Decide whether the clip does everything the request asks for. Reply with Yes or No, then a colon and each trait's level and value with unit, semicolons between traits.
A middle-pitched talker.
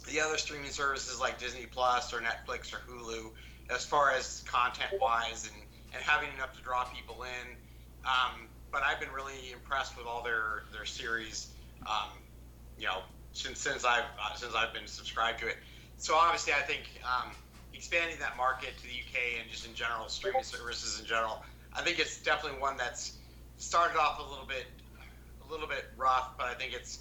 No: low, 115 Hz